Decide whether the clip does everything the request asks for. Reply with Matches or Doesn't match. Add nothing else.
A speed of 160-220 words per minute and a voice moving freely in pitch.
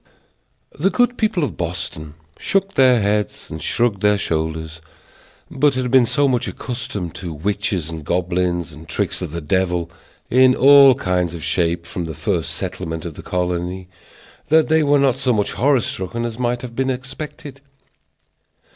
Matches